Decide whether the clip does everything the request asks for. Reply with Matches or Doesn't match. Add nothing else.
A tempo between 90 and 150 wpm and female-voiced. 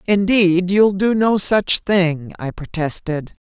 Matches